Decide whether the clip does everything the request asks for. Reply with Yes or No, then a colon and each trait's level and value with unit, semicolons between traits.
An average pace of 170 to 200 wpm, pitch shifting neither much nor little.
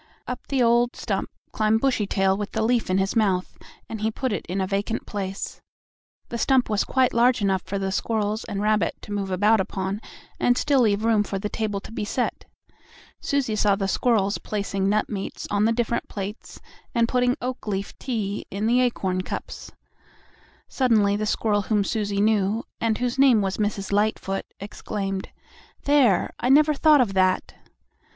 Yes: average, 180 wpm; average, 3.0 semitones